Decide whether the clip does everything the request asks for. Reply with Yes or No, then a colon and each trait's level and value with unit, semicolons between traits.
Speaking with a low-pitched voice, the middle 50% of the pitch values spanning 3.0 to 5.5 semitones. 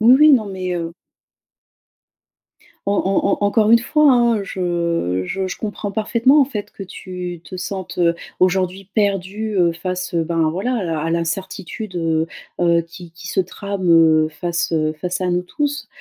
No: medium, 185 Hz; average, 3.3 semitones